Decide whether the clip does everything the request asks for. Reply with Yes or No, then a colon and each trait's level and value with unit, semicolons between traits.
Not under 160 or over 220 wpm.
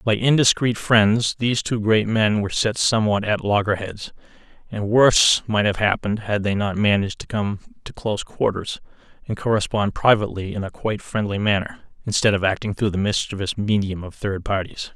Yes: average, 175 wpm